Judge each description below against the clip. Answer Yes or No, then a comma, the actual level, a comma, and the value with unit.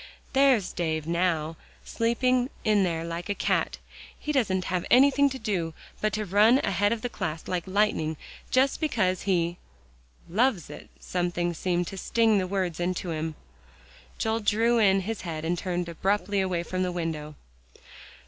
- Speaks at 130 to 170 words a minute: Yes, average, 160 wpm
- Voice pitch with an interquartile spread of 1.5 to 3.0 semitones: No, average, 4.2 semitones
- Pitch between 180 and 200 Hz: Yes, medium, 185 Hz